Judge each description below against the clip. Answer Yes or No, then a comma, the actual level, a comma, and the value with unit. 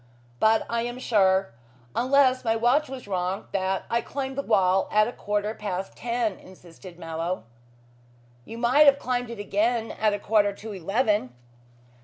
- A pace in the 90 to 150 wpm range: No, average, 160 wpm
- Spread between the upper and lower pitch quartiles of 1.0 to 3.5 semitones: No, average, 4.0 semitones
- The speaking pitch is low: No, high, 215 Hz